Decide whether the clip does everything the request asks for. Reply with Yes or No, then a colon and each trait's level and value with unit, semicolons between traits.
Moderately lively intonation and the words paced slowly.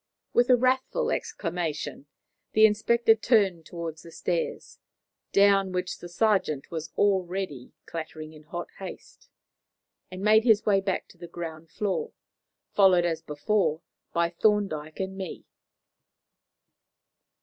Yes: average, 4.2 semitones; slow, 125 wpm